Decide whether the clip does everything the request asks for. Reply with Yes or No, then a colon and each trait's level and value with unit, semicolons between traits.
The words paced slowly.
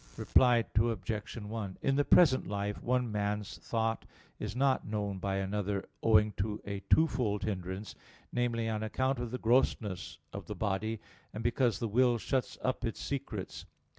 No: average, 160 wpm